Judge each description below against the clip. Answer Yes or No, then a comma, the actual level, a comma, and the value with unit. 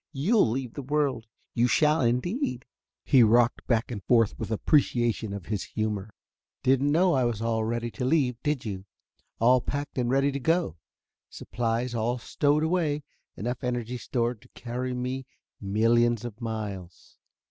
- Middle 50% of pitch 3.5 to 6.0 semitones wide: No, average, 3.1 semitones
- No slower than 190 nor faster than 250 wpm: No, average, 160 wpm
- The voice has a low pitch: Yes, low, 120 Hz